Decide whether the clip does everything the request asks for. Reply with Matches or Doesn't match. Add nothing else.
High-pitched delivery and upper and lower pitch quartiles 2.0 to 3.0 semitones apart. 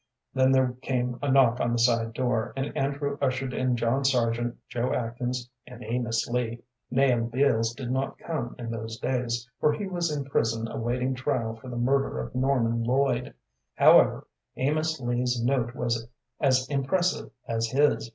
Doesn't match